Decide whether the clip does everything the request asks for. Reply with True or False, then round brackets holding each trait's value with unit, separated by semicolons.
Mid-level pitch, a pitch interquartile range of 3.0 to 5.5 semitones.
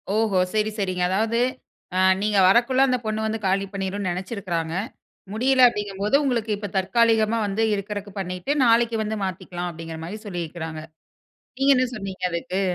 False (205 Hz; 3.3 semitones)